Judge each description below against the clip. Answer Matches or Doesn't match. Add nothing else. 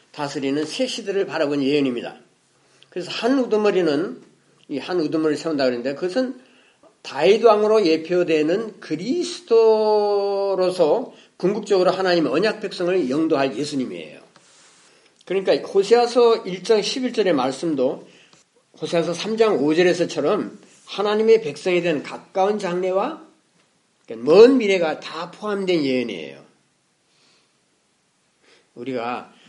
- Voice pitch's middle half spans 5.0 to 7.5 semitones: Matches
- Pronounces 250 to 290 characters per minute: Matches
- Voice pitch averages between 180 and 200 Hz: Matches